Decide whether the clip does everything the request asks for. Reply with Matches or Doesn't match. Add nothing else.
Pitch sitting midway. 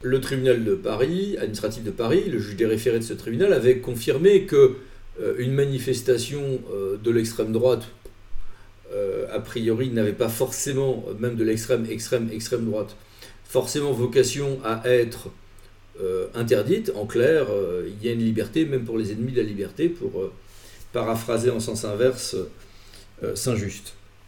Doesn't match